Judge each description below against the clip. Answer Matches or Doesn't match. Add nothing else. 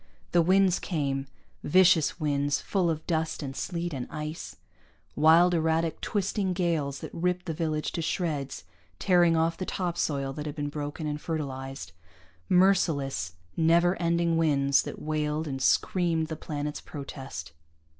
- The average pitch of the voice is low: Doesn't match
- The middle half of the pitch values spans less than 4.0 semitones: Matches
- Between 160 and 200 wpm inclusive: Doesn't match